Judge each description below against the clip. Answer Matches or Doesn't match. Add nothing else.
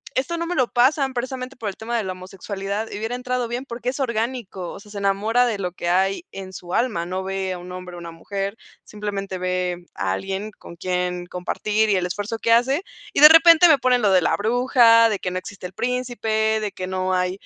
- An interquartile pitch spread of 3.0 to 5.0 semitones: Matches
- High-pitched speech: Matches